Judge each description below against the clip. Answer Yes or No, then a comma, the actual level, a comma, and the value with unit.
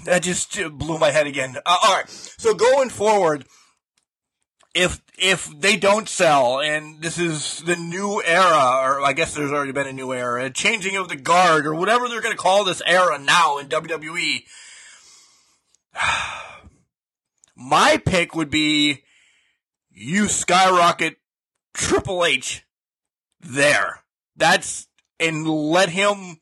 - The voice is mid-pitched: Yes, medium, 165 Hz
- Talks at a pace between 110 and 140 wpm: Yes, slow, 135 wpm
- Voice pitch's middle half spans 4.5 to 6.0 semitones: No, average, 3.8 semitones